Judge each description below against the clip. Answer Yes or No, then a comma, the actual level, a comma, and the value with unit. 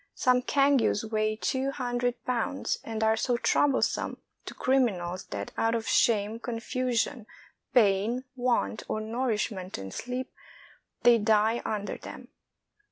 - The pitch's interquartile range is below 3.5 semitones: Yes, average, 2.7 semitones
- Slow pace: Yes, slow, 125 wpm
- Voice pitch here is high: Yes, high, 230 Hz